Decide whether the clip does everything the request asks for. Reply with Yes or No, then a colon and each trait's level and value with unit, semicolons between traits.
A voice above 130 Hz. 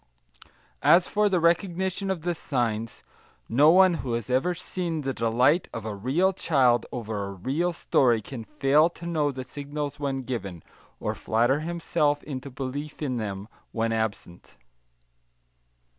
Yes: medium, 140 Hz